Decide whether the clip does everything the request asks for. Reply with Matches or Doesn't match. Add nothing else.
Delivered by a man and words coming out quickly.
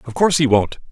Matches